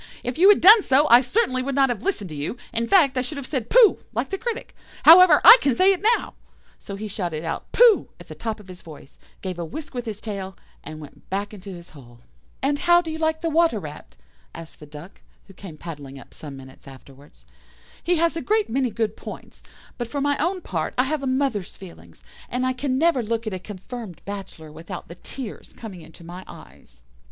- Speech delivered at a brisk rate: Yes, fast, 225 wpm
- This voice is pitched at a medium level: No, high, 225 Hz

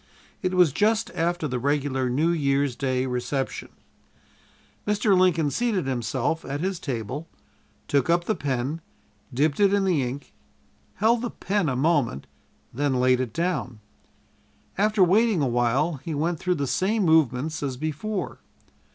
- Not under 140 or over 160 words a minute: Yes, average, 150 wpm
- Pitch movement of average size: No, wide, 5.7 semitones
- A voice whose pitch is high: No, medium, 150 Hz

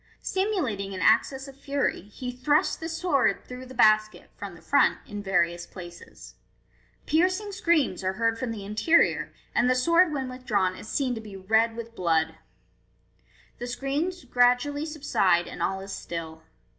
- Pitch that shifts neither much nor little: No, wide, 6.5 semitones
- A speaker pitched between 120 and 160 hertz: No, high, 245 Hz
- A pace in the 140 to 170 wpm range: Yes, average, 160 wpm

